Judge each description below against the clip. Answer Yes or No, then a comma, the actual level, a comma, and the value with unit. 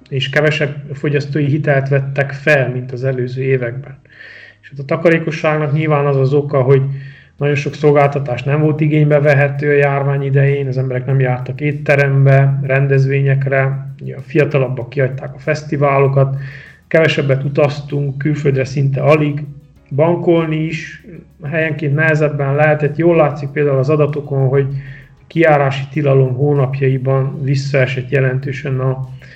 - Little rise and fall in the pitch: Yes, narrow, 1.6 semitones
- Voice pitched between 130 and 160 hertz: Yes, medium, 140 Hz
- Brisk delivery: No, average, 125 wpm